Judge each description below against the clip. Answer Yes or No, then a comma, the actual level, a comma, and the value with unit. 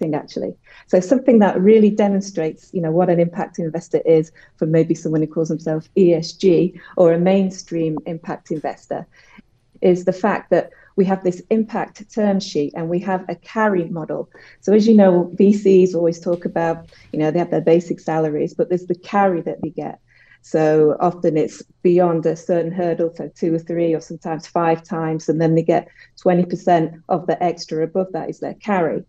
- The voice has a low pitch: No, medium, 170 Hz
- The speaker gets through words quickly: No, average, 190 wpm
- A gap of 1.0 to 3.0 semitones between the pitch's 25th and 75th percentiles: Yes, narrow, 2.4 semitones